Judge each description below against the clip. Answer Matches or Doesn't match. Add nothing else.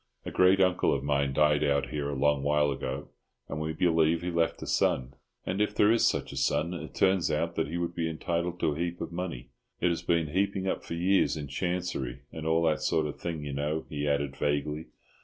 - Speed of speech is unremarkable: Doesn't match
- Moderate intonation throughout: Matches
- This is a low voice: Matches